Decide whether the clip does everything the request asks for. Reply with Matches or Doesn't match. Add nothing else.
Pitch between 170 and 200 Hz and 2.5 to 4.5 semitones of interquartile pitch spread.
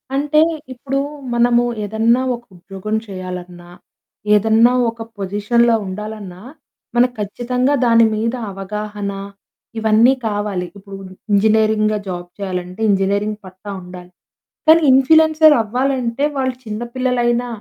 Doesn't match